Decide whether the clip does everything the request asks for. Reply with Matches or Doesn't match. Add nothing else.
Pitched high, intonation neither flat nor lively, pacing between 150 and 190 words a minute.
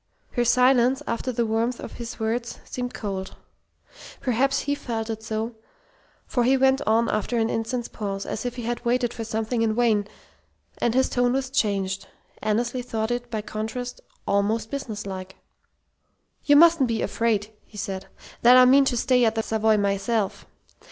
Doesn't match